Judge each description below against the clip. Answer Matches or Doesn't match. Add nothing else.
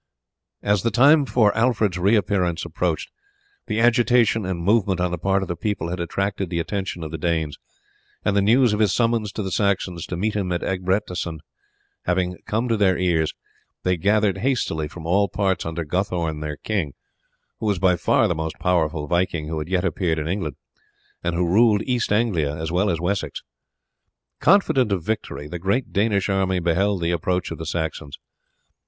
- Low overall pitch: Matches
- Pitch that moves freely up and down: Doesn't match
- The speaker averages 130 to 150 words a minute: Doesn't match